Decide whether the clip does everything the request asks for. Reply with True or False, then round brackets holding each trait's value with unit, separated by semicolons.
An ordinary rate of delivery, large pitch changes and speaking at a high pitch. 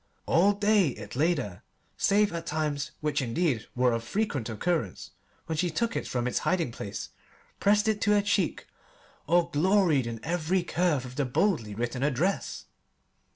False (165 wpm; 7.2 semitones; 160 Hz)